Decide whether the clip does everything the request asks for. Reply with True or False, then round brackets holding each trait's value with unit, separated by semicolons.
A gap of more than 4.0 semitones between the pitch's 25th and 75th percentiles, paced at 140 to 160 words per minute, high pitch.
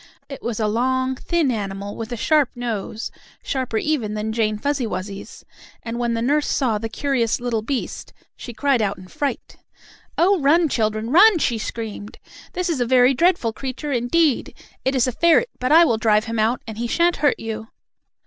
False (4.4 semitones; 190 wpm; 240 Hz)